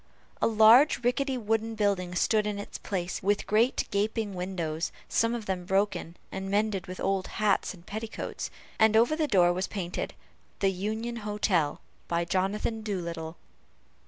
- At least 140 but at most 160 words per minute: Yes, average, 155 wpm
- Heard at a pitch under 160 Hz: No, high, 205 Hz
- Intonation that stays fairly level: No, average, 3.2 semitones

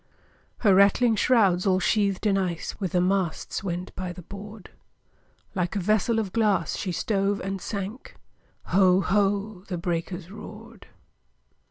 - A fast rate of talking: No, average, 145 wpm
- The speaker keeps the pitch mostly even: Yes, narrow, 2.3 semitones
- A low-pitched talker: No, high, 195 Hz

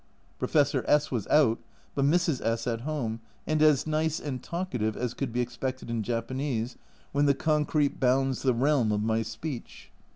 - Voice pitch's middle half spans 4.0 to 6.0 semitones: Yes, average, 4.3 semitones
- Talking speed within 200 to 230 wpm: No, average, 170 wpm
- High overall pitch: No, low, 130 Hz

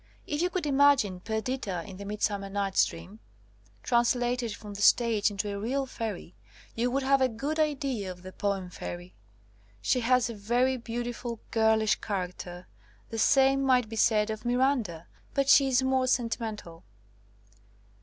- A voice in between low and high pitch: No, high, 230 Hz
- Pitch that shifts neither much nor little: Yes, average, 4.4 semitones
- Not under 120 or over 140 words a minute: No, average, 165 wpm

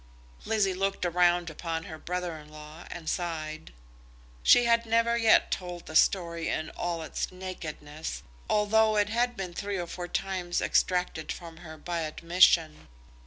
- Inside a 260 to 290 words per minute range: No, average, 155 wpm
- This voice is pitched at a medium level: Yes, medium, 175 Hz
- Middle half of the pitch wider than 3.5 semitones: No, average, 3.2 semitones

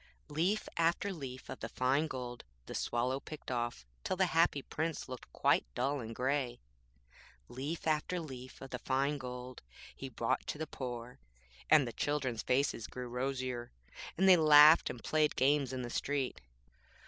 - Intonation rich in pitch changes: No, average, 3.5 semitones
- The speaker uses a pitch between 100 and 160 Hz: Yes, low, 135 Hz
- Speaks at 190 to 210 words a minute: No, average, 165 wpm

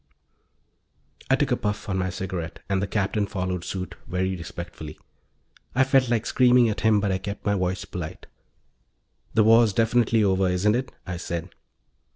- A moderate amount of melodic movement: Yes, average, 3.6 semitones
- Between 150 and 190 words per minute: Yes, average, 170 wpm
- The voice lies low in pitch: Yes, low, 100 Hz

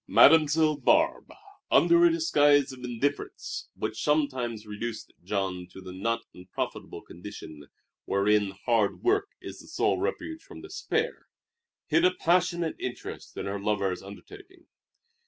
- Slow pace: Yes, slow, 130 wpm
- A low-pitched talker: Yes, low, 125 Hz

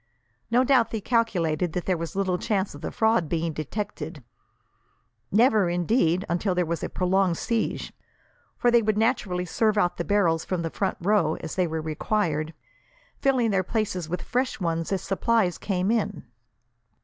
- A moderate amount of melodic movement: Yes, average, 4.5 semitones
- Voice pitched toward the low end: No, medium, 185 Hz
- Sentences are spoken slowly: No, average, 170 wpm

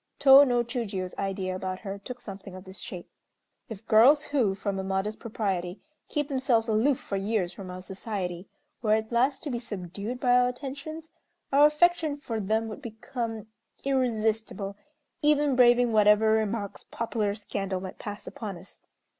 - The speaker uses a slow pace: No, average, 165 wpm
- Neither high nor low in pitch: No, high, 220 Hz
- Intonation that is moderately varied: Yes, average, 4.1 semitones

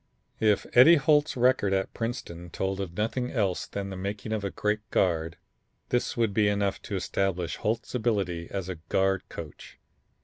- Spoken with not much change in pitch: No, average, 3.2 semitones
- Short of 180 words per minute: Yes, average, 170 wpm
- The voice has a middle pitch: No, low, 100 Hz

